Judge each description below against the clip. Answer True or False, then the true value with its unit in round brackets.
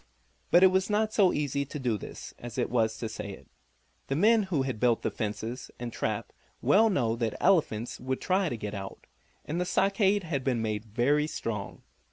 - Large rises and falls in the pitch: True (8.3 semitones)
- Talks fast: True (210 wpm)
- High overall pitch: False (130 Hz)